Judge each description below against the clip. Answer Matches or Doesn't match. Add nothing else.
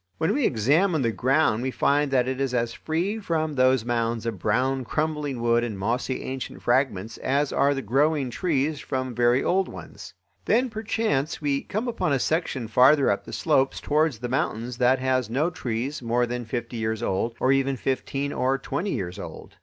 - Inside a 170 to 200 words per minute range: Matches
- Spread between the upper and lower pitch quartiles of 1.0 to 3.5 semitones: Doesn't match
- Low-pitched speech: Matches